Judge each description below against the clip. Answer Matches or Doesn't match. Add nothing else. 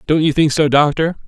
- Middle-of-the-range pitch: Matches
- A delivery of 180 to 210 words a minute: Doesn't match